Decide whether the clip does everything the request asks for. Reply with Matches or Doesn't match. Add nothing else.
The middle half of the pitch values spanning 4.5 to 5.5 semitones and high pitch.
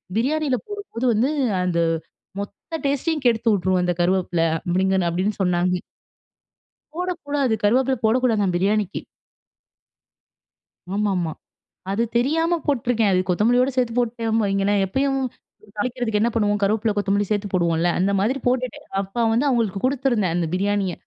Matches